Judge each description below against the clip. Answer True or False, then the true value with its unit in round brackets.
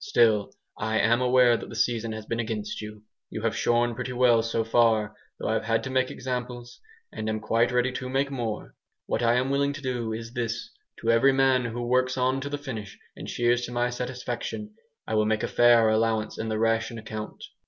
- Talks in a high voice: False (120 Hz)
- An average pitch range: False (2.2 semitones)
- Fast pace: True (215 wpm)